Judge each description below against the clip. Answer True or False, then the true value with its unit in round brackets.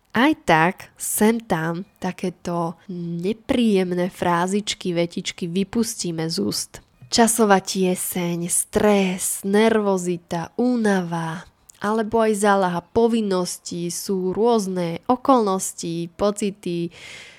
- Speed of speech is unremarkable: False (85 wpm)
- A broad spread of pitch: False (3.7 semitones)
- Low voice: False (190 Hz)